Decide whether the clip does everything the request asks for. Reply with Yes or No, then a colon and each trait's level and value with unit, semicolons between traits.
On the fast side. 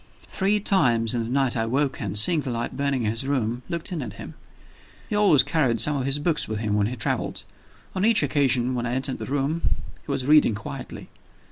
Yes: fast, 225 wpm